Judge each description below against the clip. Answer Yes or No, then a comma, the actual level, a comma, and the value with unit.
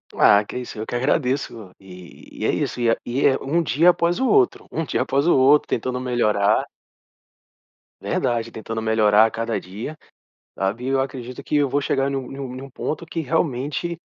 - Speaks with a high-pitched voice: No, low, 130 Hz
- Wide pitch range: No, average, 4.3 semitones